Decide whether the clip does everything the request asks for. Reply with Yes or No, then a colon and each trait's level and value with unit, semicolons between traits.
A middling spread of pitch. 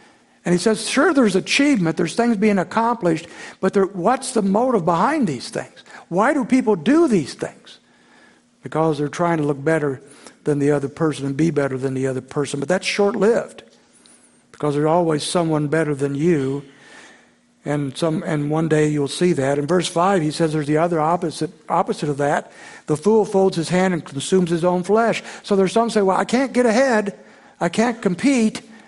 No: wide, 6.1 semitones